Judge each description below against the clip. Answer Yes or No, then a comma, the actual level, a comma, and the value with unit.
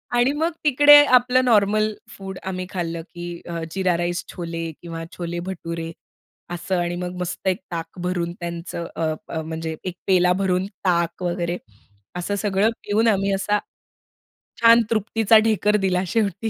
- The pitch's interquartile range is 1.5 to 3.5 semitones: Yes, average, 3.2 semitones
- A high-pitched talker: No, medium, 180 Hz